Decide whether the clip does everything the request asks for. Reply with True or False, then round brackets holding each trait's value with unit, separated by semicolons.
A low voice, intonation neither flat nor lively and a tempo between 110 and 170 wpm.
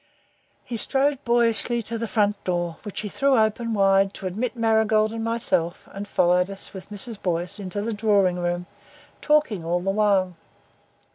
False (205 Hz; 3.6 semitones; 165 wpm)